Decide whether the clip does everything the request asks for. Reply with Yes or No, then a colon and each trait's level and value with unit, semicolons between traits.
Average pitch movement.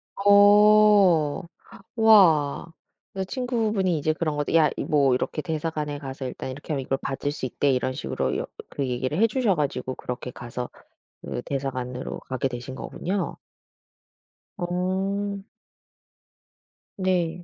No: wide, 6.5 semitones